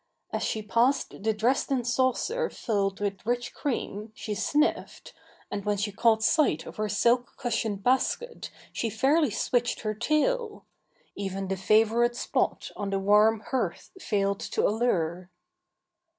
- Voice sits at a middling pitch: No, high, 220 Hz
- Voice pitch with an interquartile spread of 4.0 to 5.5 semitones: No, average, 3.4 semitones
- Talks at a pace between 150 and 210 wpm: No, average, 140 wpm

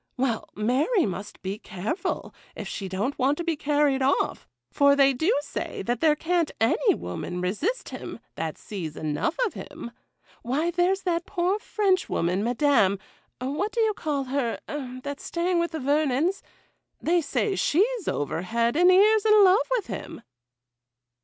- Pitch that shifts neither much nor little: No, wide, 7.3 semitones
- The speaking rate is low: No, average, 160 wpm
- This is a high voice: Yes, very high, 290 Hz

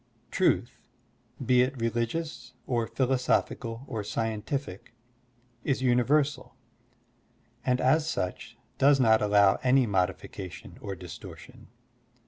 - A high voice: No, low, 120 Hz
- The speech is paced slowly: Yes, slow, 105 wpm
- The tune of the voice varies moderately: Yes, average, 4.1 semitones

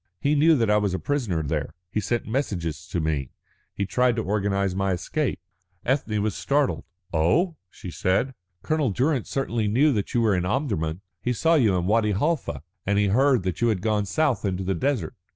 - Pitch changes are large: Yes, wide, 6.2 semitones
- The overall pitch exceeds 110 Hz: No, low, 105 Hz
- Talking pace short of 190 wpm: No, average, 200 wpm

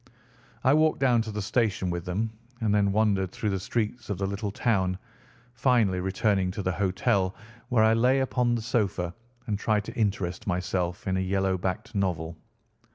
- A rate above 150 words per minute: Yes, average, 180 wpm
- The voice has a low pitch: Yes, low, 100 Hz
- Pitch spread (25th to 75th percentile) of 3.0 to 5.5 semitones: Yes, average, 3.3 semitones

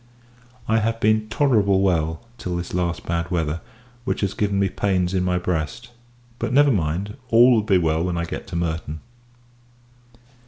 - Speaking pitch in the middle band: No, very low, 90 Hz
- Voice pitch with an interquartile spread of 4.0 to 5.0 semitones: Yes, average, 4.3 semitones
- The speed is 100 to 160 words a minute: No, average, 170 wpm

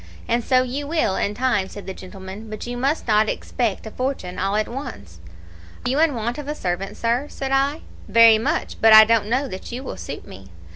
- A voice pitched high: Yes, high, 230 Hz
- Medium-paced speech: No, fast, 225 wpm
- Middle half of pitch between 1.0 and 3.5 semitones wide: No, average, 4.5 semitones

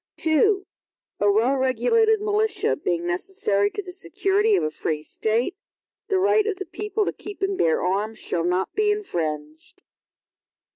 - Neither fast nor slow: Yes, average, 155 wpm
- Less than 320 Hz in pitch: No, very high, 360 Hz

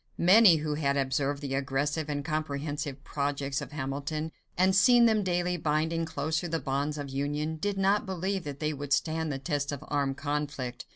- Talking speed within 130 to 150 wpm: No, average, 180 wpm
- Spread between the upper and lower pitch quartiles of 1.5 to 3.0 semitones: Yes, average, 2.7 semitones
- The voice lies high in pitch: No, medium, 150 Hz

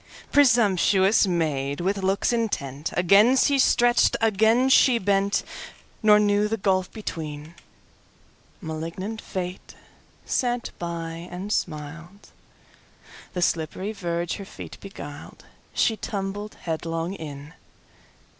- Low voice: No, high, 190 Hz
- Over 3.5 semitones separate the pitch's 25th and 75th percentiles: Yes, average, 4.4 semitones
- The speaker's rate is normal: No, slow, 90 wpm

